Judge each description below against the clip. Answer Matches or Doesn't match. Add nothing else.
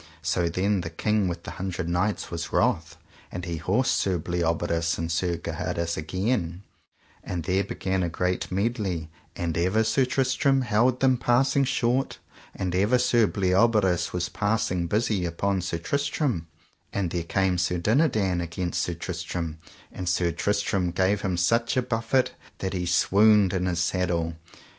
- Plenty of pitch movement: Doesn't match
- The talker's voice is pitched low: Matches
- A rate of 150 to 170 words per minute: Matches